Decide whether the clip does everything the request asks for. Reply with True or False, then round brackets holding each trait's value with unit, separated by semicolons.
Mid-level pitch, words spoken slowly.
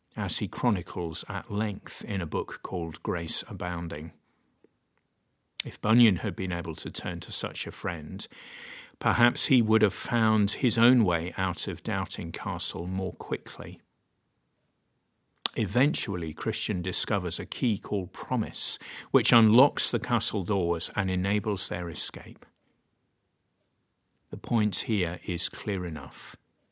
False (100 Hz; 130 wpm)